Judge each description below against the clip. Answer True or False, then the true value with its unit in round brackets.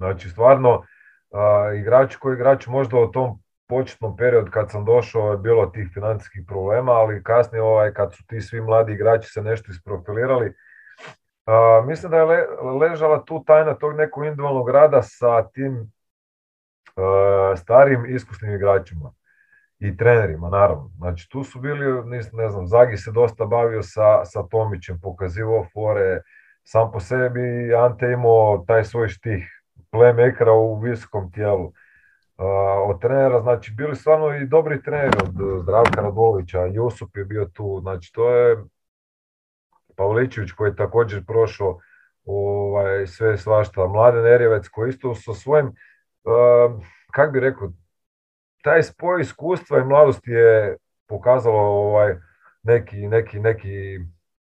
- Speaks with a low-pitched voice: True (110 Hz)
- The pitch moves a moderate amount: True (3.5 semitones)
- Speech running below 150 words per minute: True (140 wpm)